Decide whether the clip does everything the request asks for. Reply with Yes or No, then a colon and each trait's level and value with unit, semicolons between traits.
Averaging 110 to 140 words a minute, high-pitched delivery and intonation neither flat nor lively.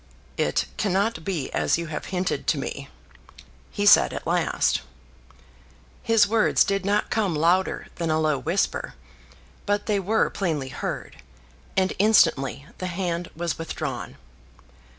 No: slow, 135 wpm; medium, 180 Hz; average, 4.0 semitones